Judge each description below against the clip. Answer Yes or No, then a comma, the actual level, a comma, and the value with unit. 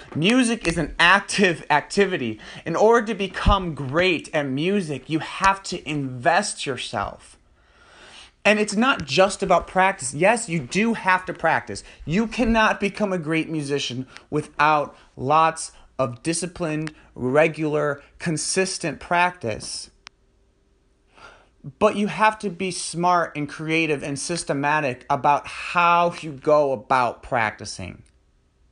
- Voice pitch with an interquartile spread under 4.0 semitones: No, average, 4.6 semitones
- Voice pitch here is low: No, medium, 165 Hz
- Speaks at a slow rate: Yes, slow, 120 wpm